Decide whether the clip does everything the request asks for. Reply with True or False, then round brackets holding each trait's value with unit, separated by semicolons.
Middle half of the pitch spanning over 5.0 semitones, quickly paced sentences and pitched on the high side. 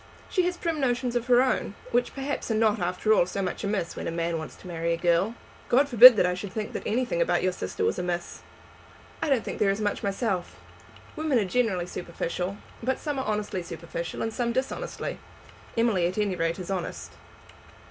True (5.6 semitones; 210 wpm; 210 Hz)